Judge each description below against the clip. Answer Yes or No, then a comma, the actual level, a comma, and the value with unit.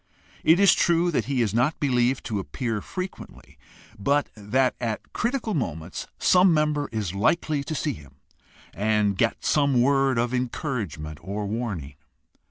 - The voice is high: No, low, 125 Hz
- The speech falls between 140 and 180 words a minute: Yes, average, 150 wpm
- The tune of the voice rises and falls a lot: Yes, wide, 6.2 semitones